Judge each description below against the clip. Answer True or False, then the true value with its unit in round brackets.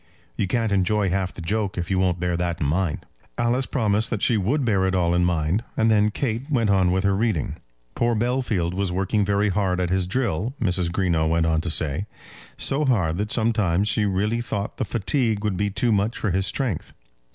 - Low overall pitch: True (100 Hz)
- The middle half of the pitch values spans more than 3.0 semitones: True (3.8 semitones)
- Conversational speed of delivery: False (215 wpm)